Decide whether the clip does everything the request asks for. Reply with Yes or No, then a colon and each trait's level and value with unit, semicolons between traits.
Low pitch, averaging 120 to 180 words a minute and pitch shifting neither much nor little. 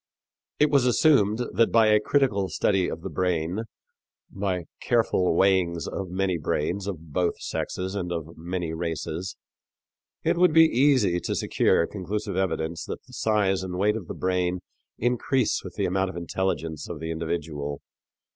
Yes: very low, 95 Hz; average, 160 wpm; average, 3.8 semitones